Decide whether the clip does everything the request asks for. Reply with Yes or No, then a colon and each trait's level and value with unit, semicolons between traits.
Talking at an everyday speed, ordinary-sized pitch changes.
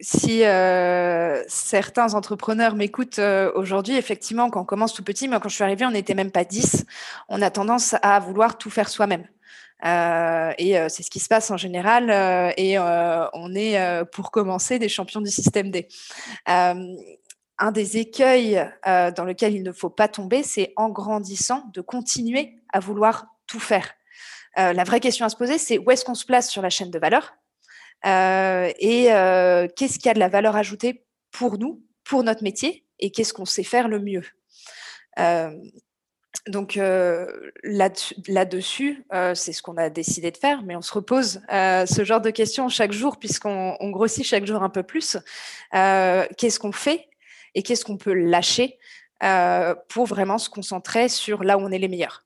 Yes: average, 195 wpm; average, 3.8 semitones